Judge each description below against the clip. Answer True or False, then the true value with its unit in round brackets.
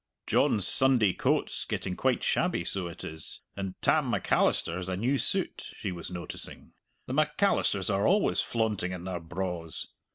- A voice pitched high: False (95 Hz)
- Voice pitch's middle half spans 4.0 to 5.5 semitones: True (4.4 semitones)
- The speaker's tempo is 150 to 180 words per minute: True (160 wpm)